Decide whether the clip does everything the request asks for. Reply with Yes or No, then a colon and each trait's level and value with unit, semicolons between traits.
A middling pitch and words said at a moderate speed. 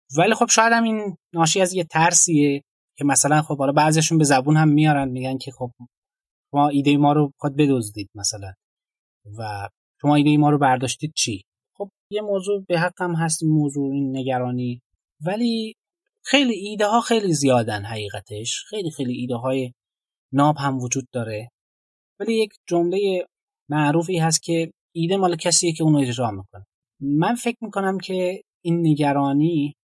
No: medium, 150 Hz; fast, 160 wpm